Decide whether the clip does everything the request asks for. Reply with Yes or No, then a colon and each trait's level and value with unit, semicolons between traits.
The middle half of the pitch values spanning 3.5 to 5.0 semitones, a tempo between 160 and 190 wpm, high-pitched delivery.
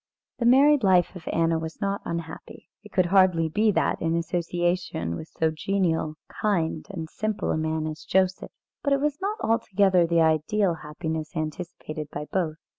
No: average, 3.8 semitones; average, 170 wpm; medium, 170 Hz